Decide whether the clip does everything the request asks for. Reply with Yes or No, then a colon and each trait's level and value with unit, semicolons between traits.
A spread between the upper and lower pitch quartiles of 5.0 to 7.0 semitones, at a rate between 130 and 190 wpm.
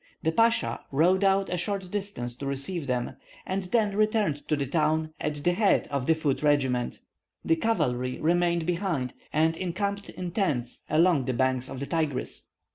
Yes: wide, 5.5 semitones; average, 175 wpm